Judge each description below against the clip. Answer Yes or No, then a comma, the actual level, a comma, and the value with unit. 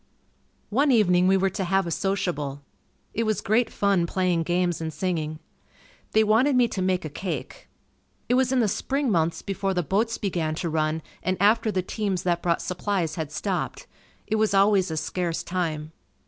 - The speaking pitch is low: No, medium, 185 Hz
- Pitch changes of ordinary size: Yes, average, 3.8 semitones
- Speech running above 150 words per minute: Yes, average, 185 wpm